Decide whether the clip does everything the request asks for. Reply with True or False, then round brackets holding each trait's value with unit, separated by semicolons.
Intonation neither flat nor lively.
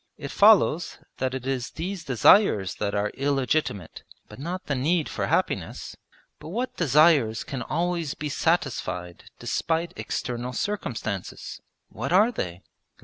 False (6.7 semitones)